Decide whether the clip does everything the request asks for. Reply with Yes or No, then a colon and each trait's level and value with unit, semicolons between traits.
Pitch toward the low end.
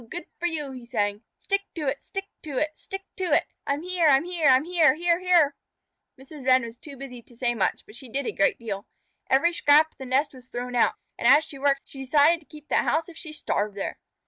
No: very high, 280 Hz